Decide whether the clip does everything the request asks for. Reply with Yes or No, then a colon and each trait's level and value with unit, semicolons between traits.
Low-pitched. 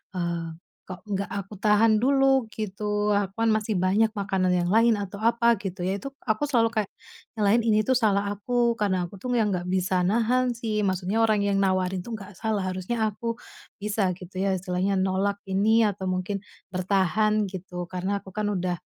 No: high, 200 Hz